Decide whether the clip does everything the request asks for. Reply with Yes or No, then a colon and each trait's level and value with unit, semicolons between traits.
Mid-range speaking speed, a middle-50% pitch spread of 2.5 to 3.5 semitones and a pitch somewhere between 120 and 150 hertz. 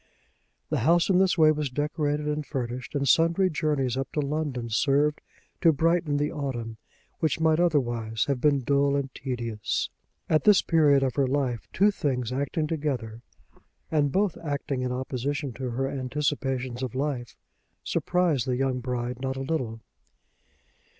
Yes: average, 155 wpm; average, 3.2 semitones; medium, 140 Hz